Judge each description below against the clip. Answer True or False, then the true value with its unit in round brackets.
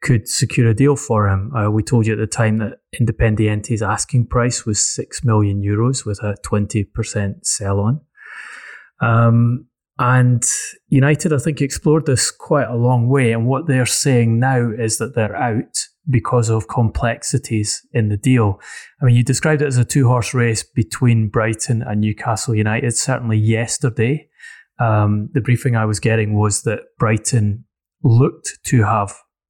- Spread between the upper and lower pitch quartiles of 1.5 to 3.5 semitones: True (2.8 semitones)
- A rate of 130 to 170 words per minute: True (165 wpm)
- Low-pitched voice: True (115 Hz)